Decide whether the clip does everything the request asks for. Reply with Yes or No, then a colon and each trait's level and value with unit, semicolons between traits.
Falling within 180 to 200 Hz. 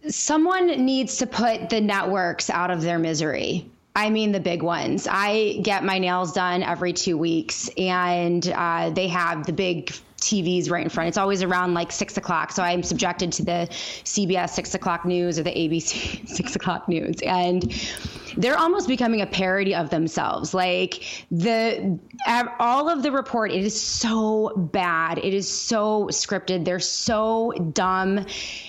Yes: medium, 185 Hz